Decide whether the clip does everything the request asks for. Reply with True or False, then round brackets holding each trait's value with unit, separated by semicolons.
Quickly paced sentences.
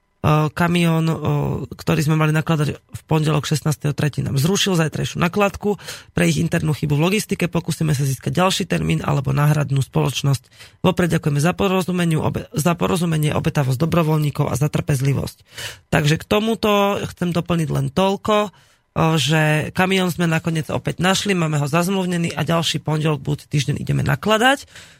False (140 wpm)